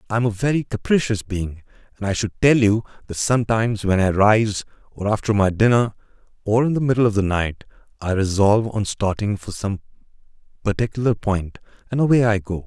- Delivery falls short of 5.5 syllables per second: No, 5.8 syllables/s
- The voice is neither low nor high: No, low, 105 Hz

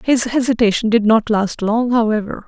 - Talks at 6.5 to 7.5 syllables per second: No, 5.1 syllables/s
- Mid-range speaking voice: No, high, 225 Hz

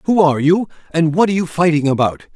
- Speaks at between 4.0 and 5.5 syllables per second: No, 6.8 syllables/s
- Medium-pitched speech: Yes, medium, 165 Hz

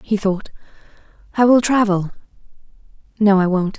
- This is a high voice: Yes, high, 205 Hz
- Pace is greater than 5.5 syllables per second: No, 5.2 syllables/s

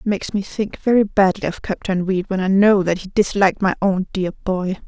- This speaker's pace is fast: Yes, fast, 235 wpm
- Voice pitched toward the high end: Yes, high, 195 Hz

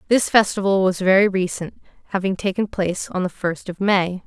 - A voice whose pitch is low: No, high, 190 Hz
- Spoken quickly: No, average, 185 wpm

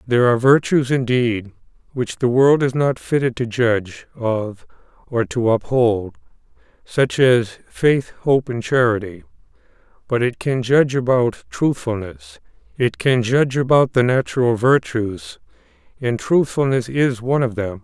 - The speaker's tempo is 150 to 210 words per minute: No, average, 140 wpm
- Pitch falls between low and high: No, low, 125 Hz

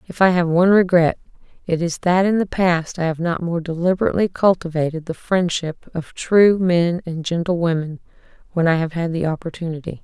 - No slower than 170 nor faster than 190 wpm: Yes, average, 185 wpm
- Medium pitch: Yes, medium, 170 Hz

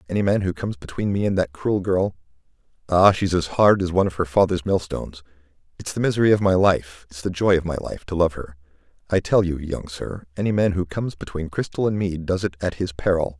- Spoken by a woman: No, male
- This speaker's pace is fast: Yes, fast, 230 wpm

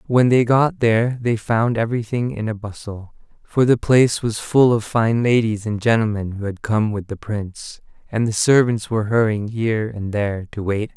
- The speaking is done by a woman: No, male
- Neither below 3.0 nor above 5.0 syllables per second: No, 5.2 syllables/s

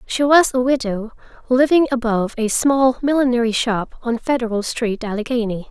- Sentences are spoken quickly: No, average, 145 wpm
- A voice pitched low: No, high, 240 Hz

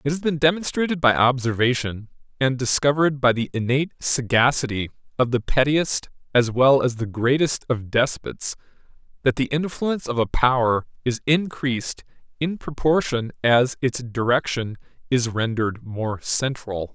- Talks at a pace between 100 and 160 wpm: Yes, average, 140 wpm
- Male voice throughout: Yes, male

